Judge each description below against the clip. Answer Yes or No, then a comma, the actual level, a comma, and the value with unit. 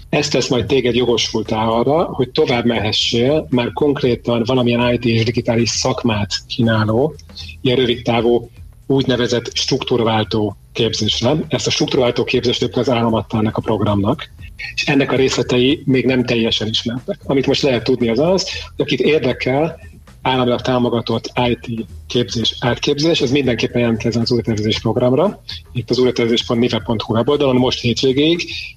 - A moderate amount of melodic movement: No, narrow, 2.2 semitones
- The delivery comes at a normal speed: Yes, average, 135 wpm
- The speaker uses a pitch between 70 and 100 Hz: No, low, 120 Hz